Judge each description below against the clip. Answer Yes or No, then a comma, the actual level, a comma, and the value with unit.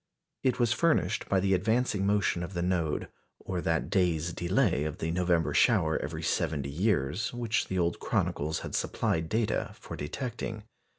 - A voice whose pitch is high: No, very low, 90 Hz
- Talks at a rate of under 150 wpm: No, average, 165 wpm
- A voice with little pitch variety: No, average, 4.7 semitones